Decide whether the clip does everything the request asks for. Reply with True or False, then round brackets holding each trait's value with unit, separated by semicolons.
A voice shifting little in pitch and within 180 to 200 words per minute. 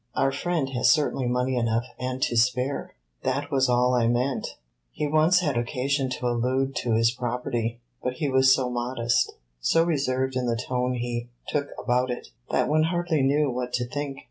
True (2.2 semitones; 185 wpm)